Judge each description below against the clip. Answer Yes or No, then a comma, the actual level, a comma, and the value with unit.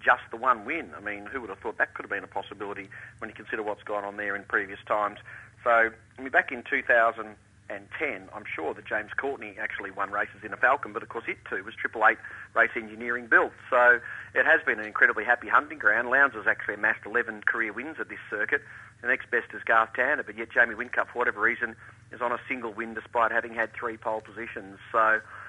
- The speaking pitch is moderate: No, low, 115 Hz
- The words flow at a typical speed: No, fast, 240 wpm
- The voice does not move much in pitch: Yes, narrow, 2.1 semitones